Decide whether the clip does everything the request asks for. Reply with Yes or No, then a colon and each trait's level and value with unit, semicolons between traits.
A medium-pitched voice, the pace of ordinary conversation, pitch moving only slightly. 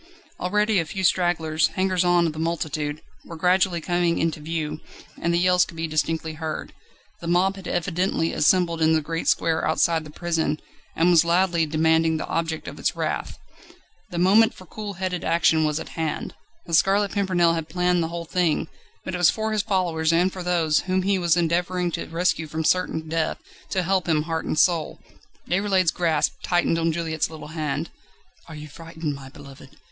Yes: medium, 170 Hz; average, 190 wpm; narrow, 2.2 semitones